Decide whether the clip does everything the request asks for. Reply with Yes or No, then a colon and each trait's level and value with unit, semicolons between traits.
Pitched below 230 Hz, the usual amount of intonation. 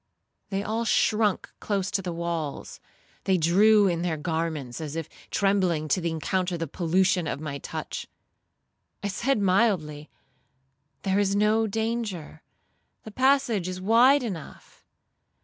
Yes: high, 190 Hz; average, 4.4 semitones